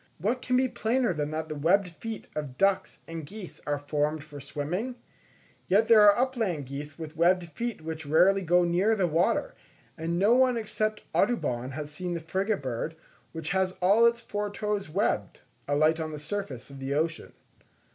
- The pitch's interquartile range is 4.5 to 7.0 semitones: Yes, wide, 5.5 semitones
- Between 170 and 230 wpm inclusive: Yes, average, 185 wpm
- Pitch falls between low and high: Yes, medium, 175 Hz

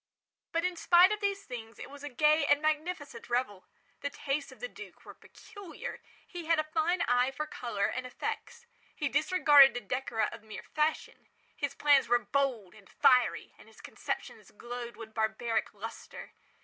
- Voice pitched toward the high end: Yes, very high, 275 Hz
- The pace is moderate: Yes, average, 175 wpm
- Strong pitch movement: No, average, 4.9 semitones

